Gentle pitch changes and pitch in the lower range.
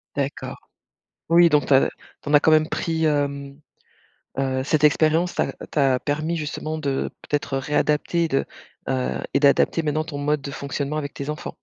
No: narrow, 1.8 semitones; medium, 150 Hz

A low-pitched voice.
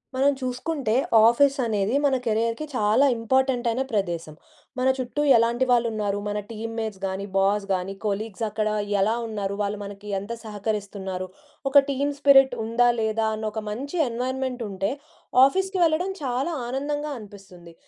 No: high, 225 Hz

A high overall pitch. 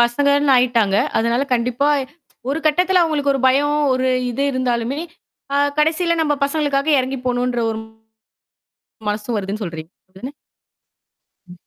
Yes: very high, 255 Hz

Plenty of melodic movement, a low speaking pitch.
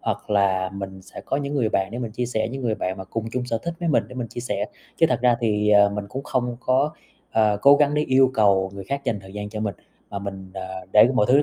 No: average, 4.5 semitones; low, 110 Hz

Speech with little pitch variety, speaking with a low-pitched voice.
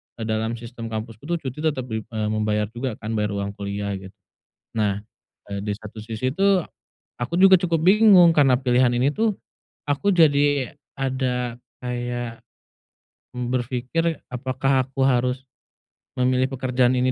No: average, 3.8 semitones; low, 125 Hz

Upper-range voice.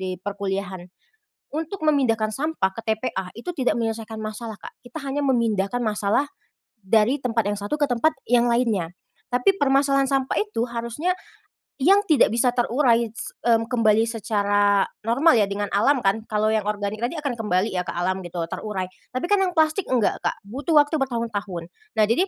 Yes: high, 230 Hz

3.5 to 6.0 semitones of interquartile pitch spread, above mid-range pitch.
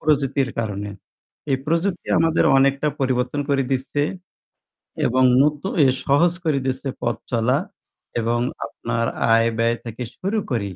No: average, 3.9 semitones; low, 130 Hz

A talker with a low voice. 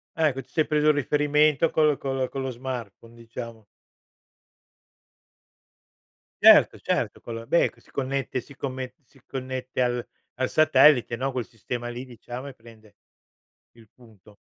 Yes: low, 130 Hz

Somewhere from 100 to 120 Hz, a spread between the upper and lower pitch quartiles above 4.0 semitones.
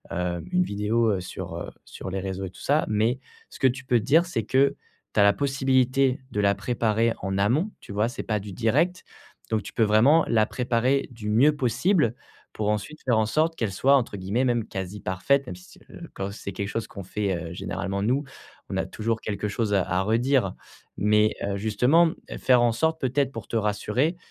Yes: low, 110 Hz; average, 4.7 semitones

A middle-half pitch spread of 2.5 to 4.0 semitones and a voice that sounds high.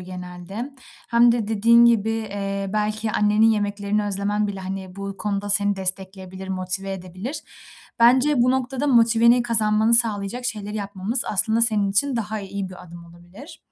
Yes: average, 3.0 semitones; high, 205 Hz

